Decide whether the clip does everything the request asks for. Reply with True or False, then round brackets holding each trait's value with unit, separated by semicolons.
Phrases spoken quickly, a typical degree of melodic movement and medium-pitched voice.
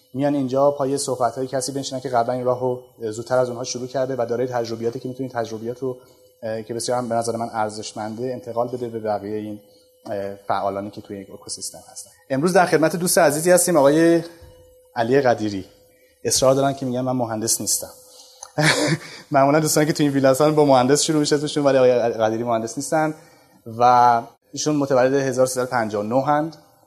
False (170 wpm; 4.0 semitones; 125 Hz)